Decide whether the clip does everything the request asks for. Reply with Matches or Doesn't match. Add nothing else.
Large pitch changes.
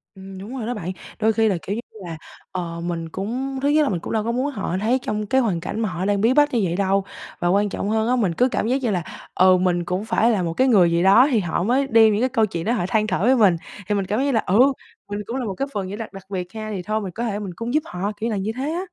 Doesn't match